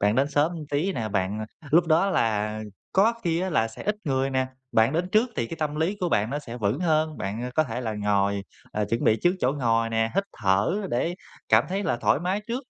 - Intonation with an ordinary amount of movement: No, wide, 7.6 semitones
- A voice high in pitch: No, low, 135 Hz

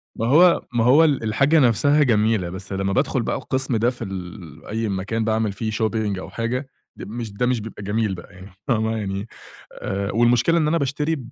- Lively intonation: No, average, 4.1 semitones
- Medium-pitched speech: No, low, 110 Hz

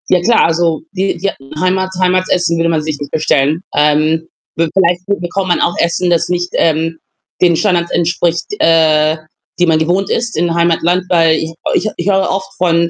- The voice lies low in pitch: No, medium, 170 Hz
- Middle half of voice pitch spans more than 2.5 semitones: No, narrow, 2.0 semitones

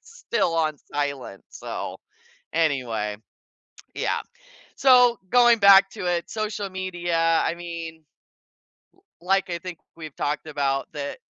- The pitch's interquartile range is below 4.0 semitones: No, average, 4.7 semitones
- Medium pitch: Yes, medium, 170 Hz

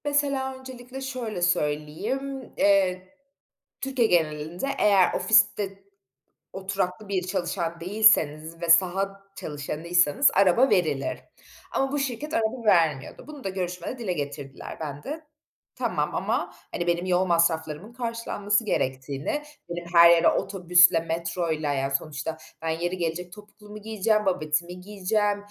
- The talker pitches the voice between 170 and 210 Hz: Yes, medium, 185 Hz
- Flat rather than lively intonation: No, average, 4.7 semitones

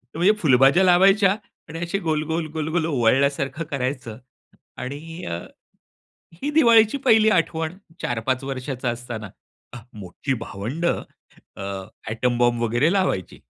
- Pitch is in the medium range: Yes, medium, 145 Hz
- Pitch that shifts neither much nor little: No, wide, 6.1 semitones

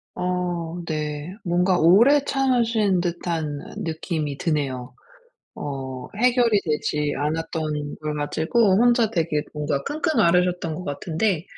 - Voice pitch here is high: No, medium, 170 Hz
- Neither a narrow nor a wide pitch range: Yes, average, 4.7 semitones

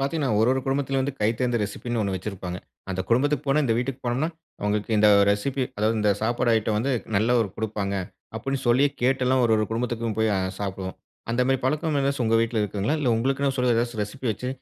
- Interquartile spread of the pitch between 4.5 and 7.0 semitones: No, average, 3.9 semitones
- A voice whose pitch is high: No, low, 120 Hz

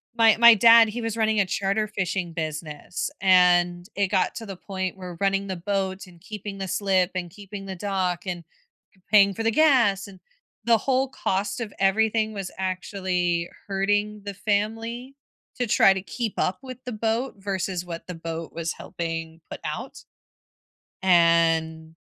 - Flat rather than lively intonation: No, average, 3.2 semitones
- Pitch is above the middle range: Yes, high, 195 Hz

